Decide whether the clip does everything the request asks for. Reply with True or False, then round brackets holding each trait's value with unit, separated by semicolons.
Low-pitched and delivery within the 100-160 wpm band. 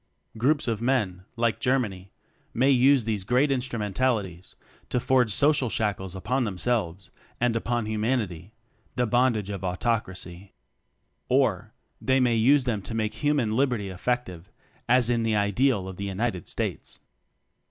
True (115 Hz; 140 wpm)